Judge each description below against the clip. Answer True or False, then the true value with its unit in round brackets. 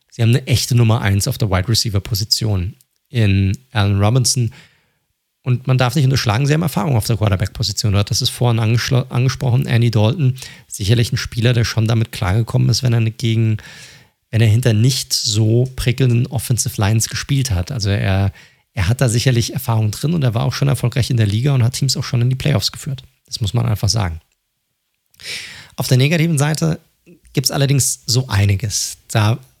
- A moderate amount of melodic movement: True (3.1 semitones)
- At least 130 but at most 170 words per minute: False (185 wpm)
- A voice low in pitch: True (120 Hz)